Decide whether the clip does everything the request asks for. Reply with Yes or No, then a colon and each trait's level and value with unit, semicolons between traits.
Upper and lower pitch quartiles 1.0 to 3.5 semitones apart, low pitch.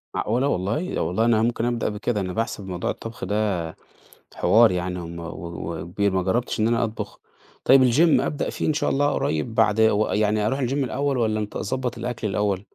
No: average, 3.9 semitones; low, 110 Hz